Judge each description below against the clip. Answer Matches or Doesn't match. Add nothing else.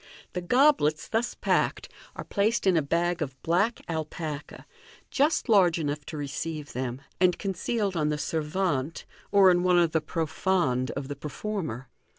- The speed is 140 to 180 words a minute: Matches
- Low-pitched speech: Doesn't match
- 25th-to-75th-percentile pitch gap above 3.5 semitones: Matches